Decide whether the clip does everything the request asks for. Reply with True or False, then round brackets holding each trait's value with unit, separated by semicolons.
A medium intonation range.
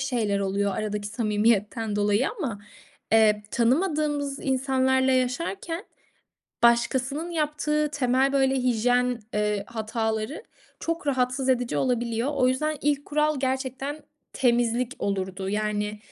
True (4.3 semitones)